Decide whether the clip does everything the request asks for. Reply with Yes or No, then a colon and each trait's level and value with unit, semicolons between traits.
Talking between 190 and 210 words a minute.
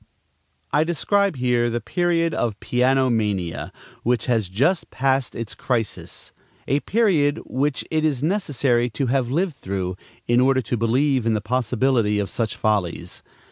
No: average, 150 wpm